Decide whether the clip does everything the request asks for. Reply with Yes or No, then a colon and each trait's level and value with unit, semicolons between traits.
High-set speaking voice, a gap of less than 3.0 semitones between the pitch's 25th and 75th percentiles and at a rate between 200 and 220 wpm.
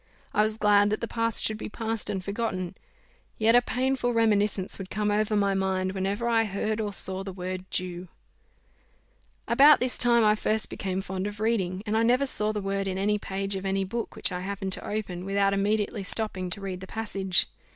Yes: high, 205 Hz; narrow, 2.4 semitones; fast, 205 wpm